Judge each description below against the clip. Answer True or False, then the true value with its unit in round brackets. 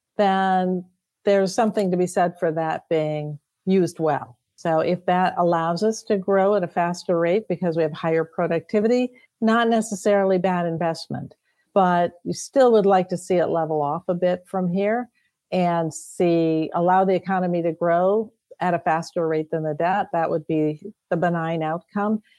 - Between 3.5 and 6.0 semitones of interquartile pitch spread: False (3.1 semitones)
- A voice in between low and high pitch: True (180 Hz)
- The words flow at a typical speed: True (175 wpm)